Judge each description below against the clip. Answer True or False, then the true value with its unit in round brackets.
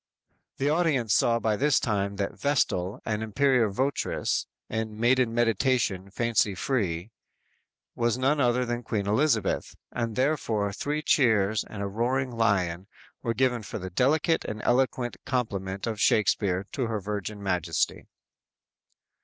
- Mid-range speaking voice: False (115 Hz)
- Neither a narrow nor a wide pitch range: True (4.2 semitones)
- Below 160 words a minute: True (145 wpm)